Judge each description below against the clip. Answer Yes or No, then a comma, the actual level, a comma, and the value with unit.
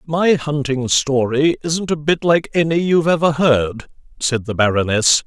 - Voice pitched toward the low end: No, medium, 145 Hz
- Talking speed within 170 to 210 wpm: No, average, 160 wpm